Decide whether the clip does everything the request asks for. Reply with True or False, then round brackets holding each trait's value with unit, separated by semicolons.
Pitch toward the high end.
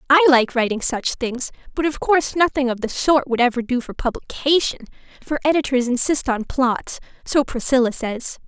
True (260 Hz)